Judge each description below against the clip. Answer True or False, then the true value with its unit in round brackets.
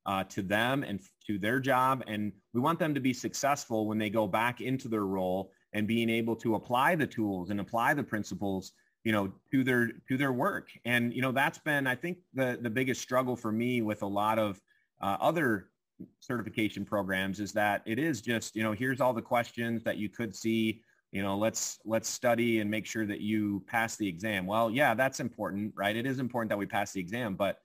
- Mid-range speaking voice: False (110 Hz)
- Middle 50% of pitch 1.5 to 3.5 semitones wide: True (3.2 semitones)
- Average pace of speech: False (225 wpm)